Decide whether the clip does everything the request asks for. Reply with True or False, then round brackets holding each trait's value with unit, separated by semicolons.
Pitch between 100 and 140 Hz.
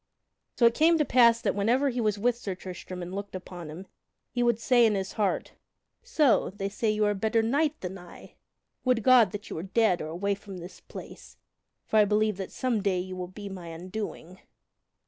False (205 Hz)